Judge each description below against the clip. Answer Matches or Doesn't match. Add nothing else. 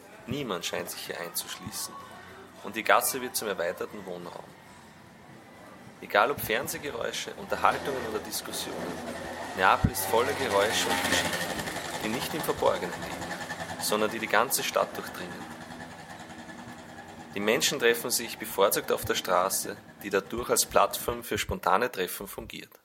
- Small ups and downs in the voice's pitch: Matches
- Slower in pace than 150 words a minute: Matches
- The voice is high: Doesn't match